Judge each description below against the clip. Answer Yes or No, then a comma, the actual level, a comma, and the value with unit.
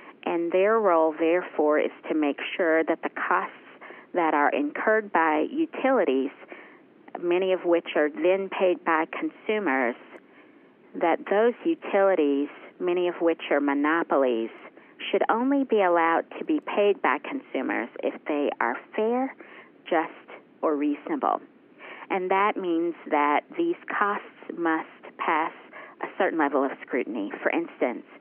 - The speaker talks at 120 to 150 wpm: Yes, slow, 135 wpm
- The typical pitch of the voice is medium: No, high, 195 Hz